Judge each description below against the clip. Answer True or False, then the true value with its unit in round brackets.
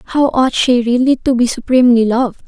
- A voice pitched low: False (245 Hz)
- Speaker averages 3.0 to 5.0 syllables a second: False (5.4 syllables/s)